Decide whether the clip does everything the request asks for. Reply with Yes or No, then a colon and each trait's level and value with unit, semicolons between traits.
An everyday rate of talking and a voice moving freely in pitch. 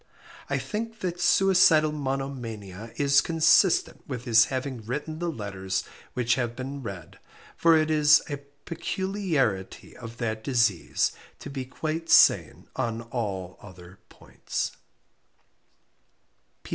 No: slow, 120 wpm; wide, 5.8 semitones